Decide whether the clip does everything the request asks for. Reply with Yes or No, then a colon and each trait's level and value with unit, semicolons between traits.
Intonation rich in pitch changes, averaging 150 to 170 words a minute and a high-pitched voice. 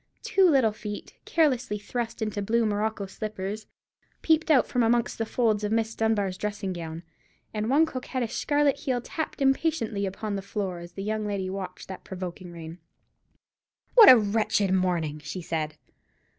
No: average, 4.2 semitones; average, 160 wpm; high, 215 Hz